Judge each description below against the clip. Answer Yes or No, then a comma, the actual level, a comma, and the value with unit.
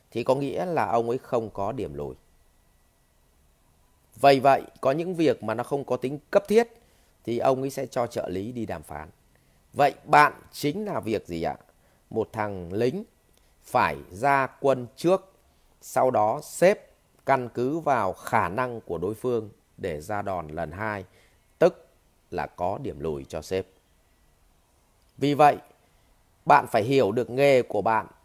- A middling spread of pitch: No, wide, 7.8 semitones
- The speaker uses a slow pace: No, average, 165 wpm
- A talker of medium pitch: No, low, 110 Hz